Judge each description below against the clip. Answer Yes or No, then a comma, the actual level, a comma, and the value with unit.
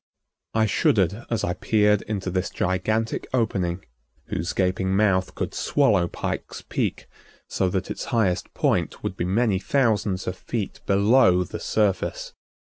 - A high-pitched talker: No, low, 100 Hz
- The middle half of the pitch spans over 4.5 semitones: No, average, 3.0 semitones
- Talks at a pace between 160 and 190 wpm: No, average, 140 wpm